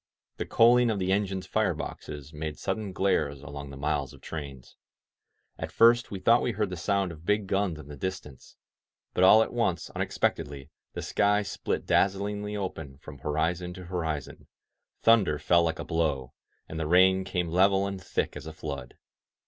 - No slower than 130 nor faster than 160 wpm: No, average, 180 wpm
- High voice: No, very low, 90 Hz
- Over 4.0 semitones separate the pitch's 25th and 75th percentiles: Yes, average, 4.6 semitones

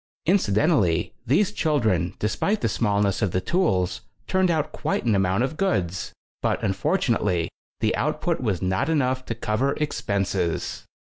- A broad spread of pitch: Yes, wide, 8.4 semitones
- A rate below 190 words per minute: Yes, average, 140 wpm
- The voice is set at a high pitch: No, low, 110 Hz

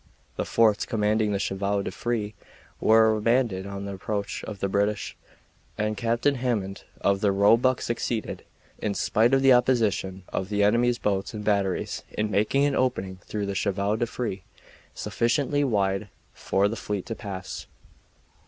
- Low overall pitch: Yes, low, 105 Hz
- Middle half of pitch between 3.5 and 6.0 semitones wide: No, average, 3.0 semitones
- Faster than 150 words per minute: Yes, average, 160 wpm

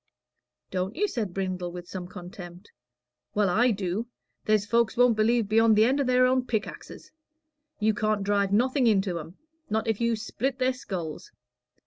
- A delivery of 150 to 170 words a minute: Yes, average, 165 wpm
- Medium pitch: No, high, 215 Hz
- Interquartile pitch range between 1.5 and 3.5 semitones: No, average, 3.9 semitones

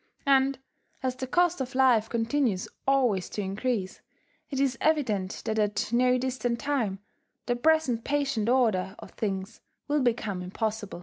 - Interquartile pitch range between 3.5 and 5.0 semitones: Yes, average, 4.3 semitones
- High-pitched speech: Yes, high, 245 Hz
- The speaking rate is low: No, average, 145 wpm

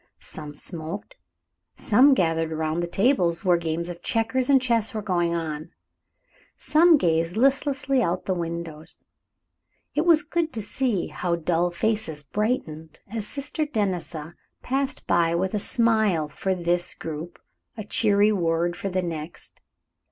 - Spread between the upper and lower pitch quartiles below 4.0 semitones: No, wide, 5.5 semitones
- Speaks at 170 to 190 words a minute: No, average, 145 wpm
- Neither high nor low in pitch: Yes, medium, 180 Hz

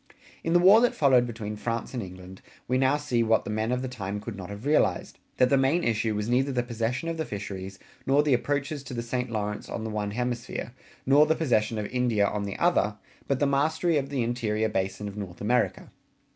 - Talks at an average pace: No, fast, 225 wpm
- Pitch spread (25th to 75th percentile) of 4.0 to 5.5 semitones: Yes, average, 4.5 semitones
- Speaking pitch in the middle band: No, low, 120 Hz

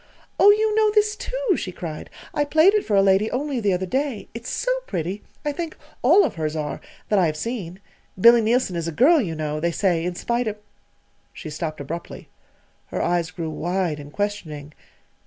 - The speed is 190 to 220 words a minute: Yes, fast, 205 wpm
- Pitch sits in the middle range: No, high, 195 Hz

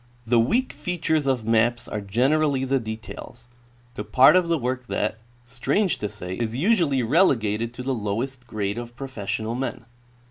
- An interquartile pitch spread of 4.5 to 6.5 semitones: No, average, 3.8 semitones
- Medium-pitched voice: No, low, 120 Hz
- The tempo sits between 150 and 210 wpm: Yes, average, 165 wpm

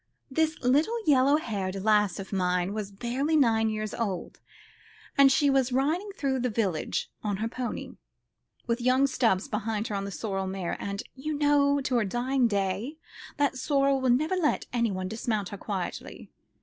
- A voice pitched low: No, high, 235 Hz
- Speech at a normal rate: Yes, average, 170 wpm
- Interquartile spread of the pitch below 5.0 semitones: No, average, 5.3 semitones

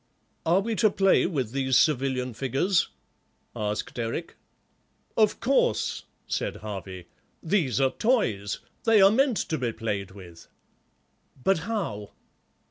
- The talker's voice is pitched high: No, low, 135 Hz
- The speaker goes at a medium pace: No, slow, 125 wpm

